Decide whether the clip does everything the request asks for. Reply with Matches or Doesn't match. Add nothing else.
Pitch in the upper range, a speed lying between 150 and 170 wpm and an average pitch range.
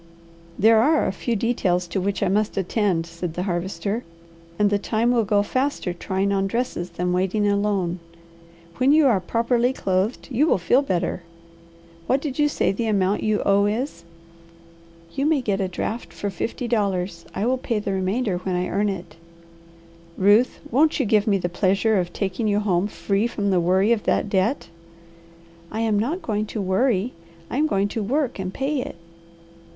Doesn't match